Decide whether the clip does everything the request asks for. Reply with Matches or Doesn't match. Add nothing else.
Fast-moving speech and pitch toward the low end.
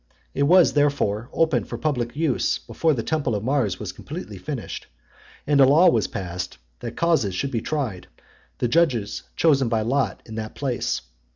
Doesn't match